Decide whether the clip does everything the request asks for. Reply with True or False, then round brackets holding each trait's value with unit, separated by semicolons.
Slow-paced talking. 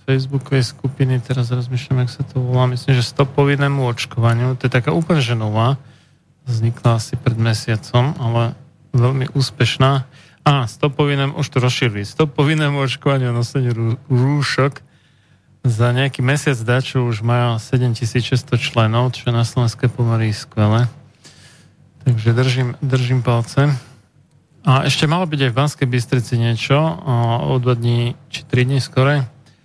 False (140 wpm)